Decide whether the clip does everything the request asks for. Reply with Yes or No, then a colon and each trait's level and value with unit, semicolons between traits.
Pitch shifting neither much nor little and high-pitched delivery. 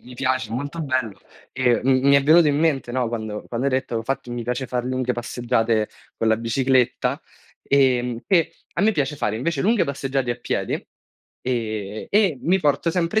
No: average, 3.0 semitones; low, 130 Hz